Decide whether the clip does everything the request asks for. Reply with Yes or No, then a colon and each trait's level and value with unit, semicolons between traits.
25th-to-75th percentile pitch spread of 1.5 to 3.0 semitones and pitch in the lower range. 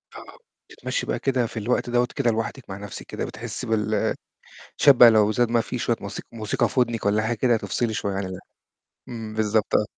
Yes: narrow, 2.4 semitones; low, 115 Hz